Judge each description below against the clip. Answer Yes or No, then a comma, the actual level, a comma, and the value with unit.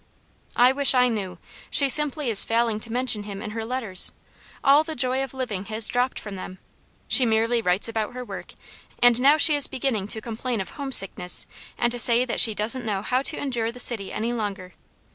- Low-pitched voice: No, high, 235 Hz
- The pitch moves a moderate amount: Yes, average, 3.3 semitones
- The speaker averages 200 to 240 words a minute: Yes, fast, 205 wpm